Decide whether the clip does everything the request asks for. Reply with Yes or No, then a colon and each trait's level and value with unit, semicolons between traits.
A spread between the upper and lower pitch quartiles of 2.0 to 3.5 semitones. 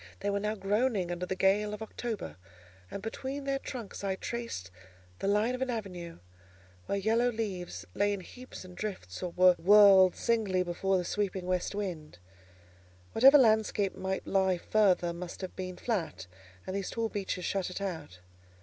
Yes: average, 3.2 semitones